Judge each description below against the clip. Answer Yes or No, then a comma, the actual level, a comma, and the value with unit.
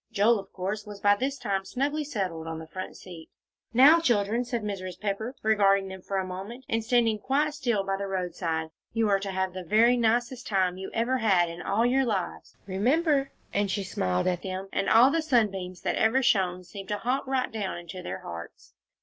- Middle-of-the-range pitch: No, high, 205 Hz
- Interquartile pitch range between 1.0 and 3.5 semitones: No, average, 4.3 semitones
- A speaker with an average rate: No, fast, 210 wpm